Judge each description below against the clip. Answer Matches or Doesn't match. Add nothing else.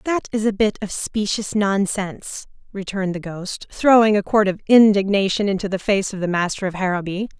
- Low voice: Doesn't match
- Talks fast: Doesn't match